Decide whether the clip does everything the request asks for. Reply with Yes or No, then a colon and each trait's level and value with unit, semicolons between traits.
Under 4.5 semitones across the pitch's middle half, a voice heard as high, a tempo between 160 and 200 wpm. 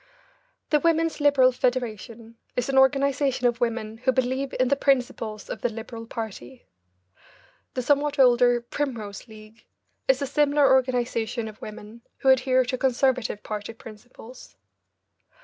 No: average, 2.9 semitones; very high, 250 Hz; slow, 135 wpm